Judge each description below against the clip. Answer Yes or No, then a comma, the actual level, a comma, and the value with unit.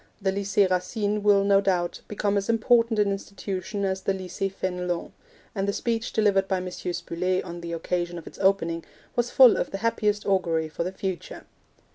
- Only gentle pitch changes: Yes, narrow, 2.2 semitones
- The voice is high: Yes, high, 195 Hz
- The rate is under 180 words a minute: No, average, 185 wpm